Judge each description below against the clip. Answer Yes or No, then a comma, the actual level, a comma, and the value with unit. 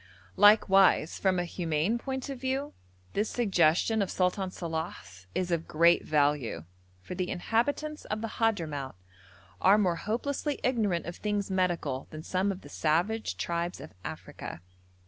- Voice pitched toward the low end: No, medium, 185 Hz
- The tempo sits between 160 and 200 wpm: No, average, 145 wpm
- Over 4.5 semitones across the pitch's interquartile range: Yes, average, 5.2 semitones